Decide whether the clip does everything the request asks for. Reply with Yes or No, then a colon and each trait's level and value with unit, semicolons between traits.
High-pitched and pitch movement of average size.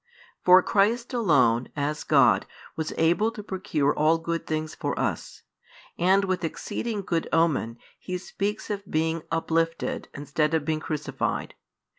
No: medium, 165 Hz; average, 3.6 semitones